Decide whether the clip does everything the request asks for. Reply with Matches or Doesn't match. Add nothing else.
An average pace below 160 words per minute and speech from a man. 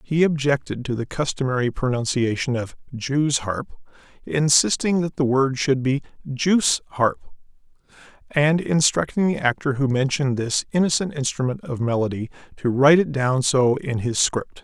Matches